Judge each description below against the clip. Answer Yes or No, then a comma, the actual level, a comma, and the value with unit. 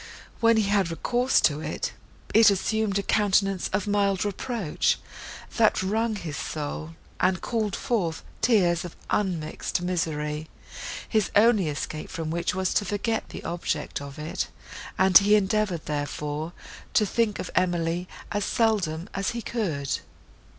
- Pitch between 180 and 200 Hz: Yes, high, 190 Hz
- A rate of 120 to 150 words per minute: Yes, average, 145 wpm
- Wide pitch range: No, average, 4.5 semitones